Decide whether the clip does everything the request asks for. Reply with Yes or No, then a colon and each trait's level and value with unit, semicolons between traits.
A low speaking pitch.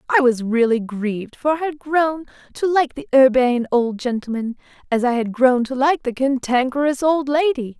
No: very high, 265 Hz